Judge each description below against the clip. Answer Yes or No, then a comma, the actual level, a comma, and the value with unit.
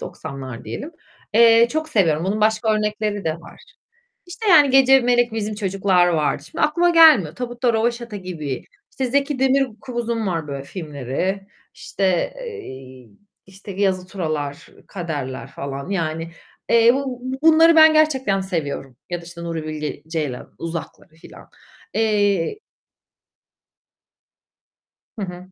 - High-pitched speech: Yes, high, 195 Hz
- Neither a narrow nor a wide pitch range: No, wide, 7.0 semitones